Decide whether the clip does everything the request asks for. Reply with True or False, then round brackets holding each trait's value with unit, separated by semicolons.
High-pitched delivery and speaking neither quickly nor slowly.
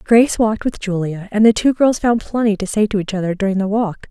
False (210 Hz; 265 wpm)